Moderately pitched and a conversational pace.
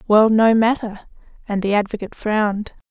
No: high, 215 Hz; average, 145 wpm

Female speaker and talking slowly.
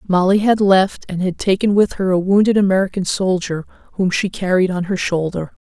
No: female; average, 190 wpm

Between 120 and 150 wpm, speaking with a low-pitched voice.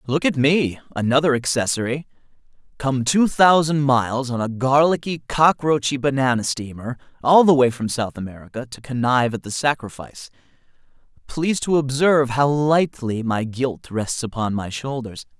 Yes: average, 140 wpm; low, 130 Hz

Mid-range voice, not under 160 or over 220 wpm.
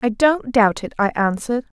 No: high, 230 Hz; average, 200 wpm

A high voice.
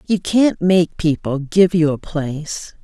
No: medium, 165 Hz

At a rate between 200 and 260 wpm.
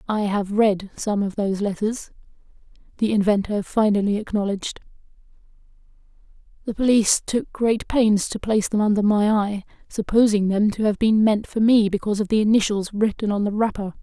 No: average, 165 wpm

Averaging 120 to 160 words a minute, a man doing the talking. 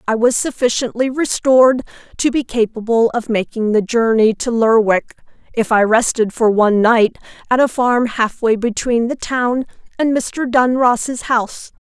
No: average, 150 wpm; female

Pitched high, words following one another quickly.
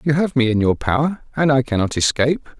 No: low, 135 Hz; fast, 230 wpm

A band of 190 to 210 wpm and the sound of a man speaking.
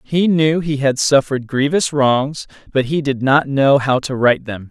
Yes: fast, 205 wpm; male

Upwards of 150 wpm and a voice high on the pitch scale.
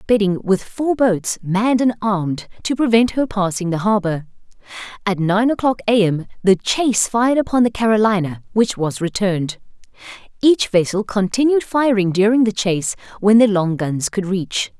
Yes: average, 160 wpm; high, 205 Hz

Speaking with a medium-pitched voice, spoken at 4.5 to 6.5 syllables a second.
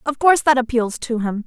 No: very high, 250 Hz; 5.9 syllables/s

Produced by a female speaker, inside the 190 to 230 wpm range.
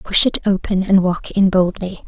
Yes: female; average, 200 wpm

